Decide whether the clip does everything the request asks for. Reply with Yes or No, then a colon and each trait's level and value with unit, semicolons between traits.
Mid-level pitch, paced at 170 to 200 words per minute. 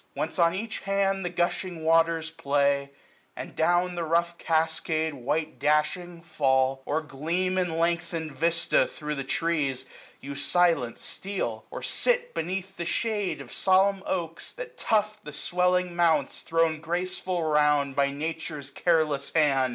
No: medium, 165 Hz; average, 145 wpm